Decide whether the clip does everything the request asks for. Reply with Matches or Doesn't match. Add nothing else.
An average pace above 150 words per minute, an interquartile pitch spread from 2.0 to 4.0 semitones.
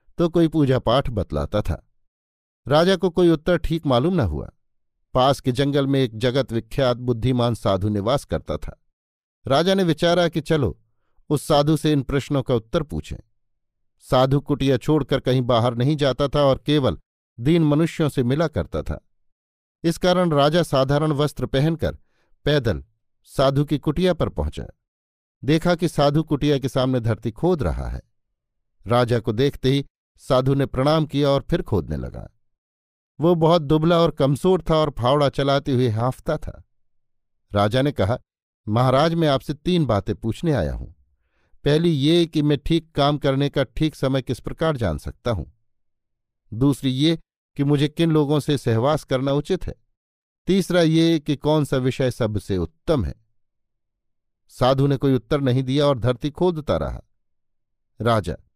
Doesn't match